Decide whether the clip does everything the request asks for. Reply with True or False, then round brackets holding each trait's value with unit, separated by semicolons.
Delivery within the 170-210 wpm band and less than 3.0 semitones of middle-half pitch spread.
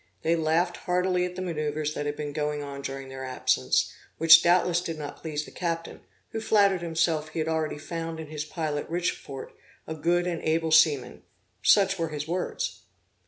True (185 wpm; 2.6 semitones)